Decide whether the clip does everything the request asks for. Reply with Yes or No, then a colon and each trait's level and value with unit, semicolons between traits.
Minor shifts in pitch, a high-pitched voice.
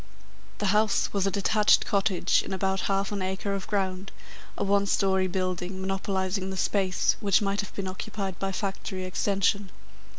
Yes: narrow, 1.1 semitones; high, 195 Hz